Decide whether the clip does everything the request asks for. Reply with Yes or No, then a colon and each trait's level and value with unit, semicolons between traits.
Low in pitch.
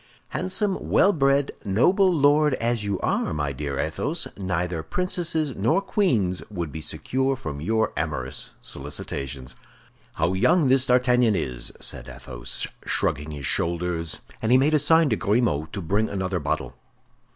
Yes: low, 105 Hz